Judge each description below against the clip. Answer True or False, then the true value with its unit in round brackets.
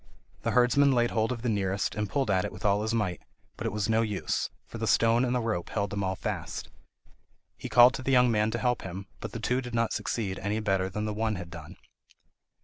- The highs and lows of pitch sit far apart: False (3.3 semitones)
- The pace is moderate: False (245 wpm)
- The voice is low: True (110 Hz)